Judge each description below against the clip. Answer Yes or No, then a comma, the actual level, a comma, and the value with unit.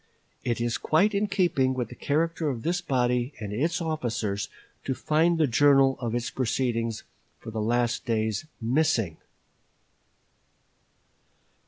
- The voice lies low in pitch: Yes, low, 130 Hz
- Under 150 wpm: Yes, slow, 135 wpm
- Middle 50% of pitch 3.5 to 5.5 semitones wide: Yes, average, 5.2 semitones